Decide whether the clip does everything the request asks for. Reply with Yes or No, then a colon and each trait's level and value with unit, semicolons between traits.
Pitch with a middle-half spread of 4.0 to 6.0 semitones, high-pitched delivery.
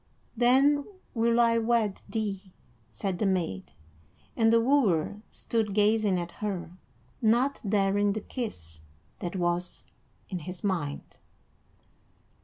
Yes: average, 4.3 semitones; high, 205 Hz